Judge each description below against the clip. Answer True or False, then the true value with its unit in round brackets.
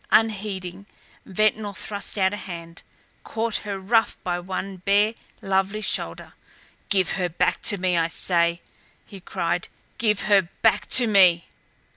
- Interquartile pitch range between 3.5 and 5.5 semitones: False (2.9 semitones)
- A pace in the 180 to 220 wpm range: False (140 wpm)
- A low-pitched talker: False (195 Hz)